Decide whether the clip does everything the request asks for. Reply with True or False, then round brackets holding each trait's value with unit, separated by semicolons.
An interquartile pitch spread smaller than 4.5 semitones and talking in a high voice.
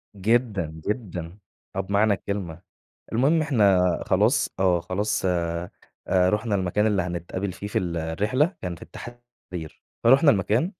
False (4.0 semitones; 100 Hz)